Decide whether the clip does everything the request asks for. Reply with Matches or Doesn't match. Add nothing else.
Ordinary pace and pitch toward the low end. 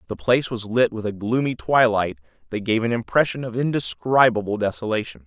Matches